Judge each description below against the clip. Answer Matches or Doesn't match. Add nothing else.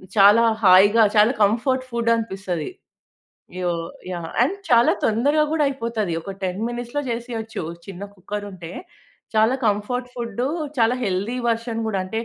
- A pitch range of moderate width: Matches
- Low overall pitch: Doesn't match